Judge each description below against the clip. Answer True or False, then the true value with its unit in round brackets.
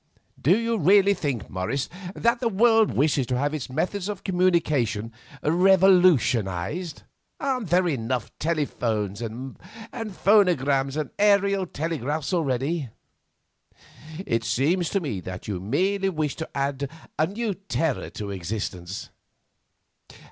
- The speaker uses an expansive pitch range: True (7.3 semitones)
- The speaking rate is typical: False (120 wpm)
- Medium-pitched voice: True (155 Hz)